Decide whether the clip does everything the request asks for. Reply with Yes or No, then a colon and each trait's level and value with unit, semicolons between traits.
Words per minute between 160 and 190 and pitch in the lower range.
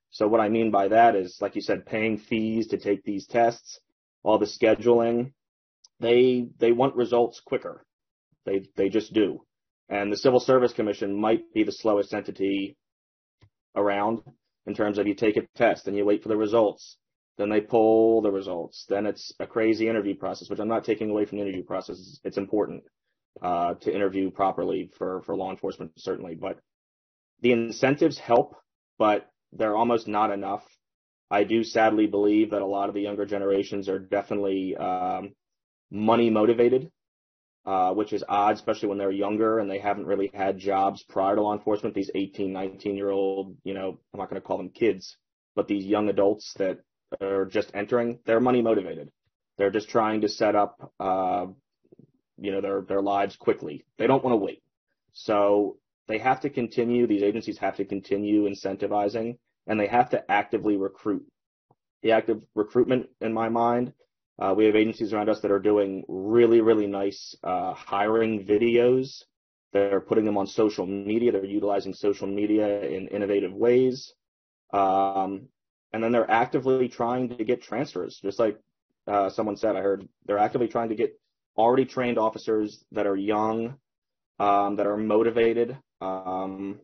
Yes: average, 175 wpm; low, 105 Hz